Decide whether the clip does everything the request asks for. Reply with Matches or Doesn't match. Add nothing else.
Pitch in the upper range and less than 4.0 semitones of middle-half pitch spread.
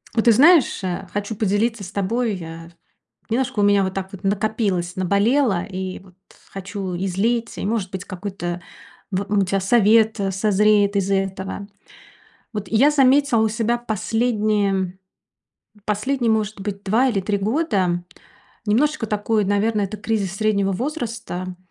Matches